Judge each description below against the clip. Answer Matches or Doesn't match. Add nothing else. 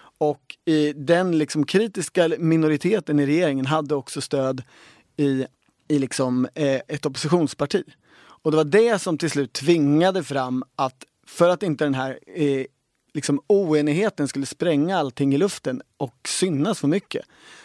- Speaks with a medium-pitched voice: Matches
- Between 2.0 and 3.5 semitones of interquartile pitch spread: Matches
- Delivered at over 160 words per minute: Doesn't match